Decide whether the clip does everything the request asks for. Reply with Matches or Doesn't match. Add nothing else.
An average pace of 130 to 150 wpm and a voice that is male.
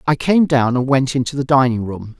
Doesn't match